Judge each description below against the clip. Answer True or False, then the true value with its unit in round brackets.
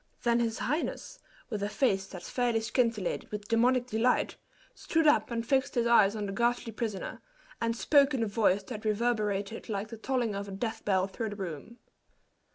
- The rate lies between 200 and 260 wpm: False (185 wpm)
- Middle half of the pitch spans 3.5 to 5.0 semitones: False (2.9 semitones)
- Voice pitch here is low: False (225 Hz)